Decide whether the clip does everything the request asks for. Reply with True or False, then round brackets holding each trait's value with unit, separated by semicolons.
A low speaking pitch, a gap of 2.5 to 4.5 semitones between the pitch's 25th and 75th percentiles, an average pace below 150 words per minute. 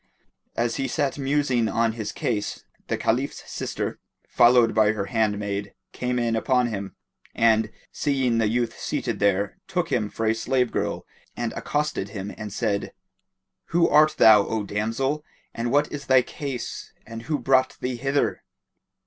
False (120 Hz; 3.7 semitones; 155 wpm)